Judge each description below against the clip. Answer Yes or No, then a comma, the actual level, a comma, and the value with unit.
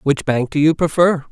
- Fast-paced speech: Yes, fast, 230 wpm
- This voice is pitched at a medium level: Yes, medium, 150 Hz